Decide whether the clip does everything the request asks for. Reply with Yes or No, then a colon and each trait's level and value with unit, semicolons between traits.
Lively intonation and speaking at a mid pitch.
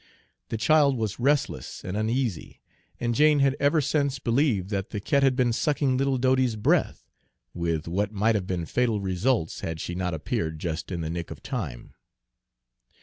No: wide, 6.8 semitones; low, 110 Hz